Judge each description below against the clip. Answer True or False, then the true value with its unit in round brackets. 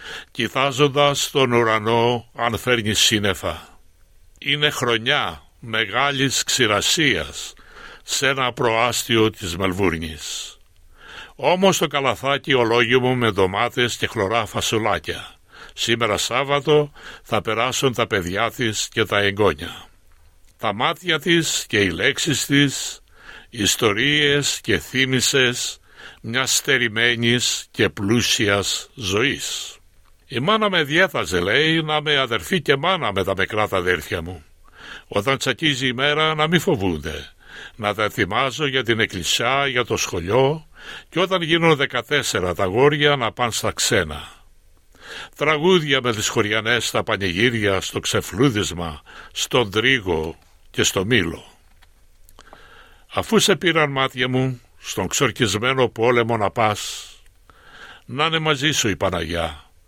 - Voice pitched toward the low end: True (120 Hz)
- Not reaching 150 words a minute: True (120 wpm)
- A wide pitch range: True (6.3 semitones)